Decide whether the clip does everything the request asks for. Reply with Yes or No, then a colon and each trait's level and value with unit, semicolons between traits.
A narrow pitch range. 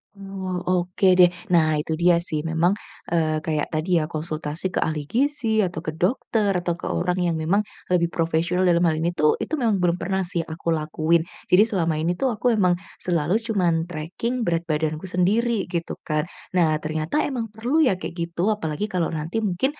No: average, 3.2 semitones